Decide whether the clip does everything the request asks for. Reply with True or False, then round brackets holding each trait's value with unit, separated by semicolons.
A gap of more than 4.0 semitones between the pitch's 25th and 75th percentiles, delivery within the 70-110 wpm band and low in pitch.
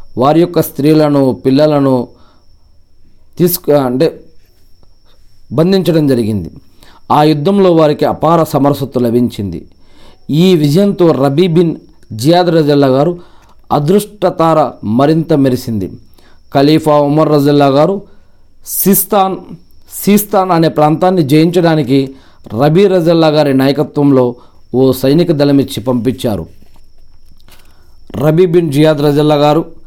False (5.5 semitones; 90 wpm; 145 Hz)